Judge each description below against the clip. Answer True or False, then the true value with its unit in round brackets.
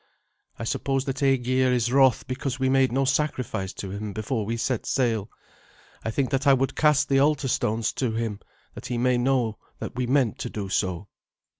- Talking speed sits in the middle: True (195 wpm)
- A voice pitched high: False (125 Hz)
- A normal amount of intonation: True (3.3 semitones)